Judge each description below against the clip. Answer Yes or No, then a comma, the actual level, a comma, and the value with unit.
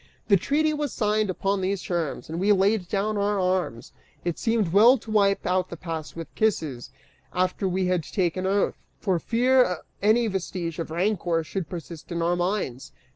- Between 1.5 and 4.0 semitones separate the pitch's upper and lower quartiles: Yes, average, 3.5 semitones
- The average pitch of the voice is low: No, medium, 185 Hz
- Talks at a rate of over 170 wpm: Yes, average, 180 wpm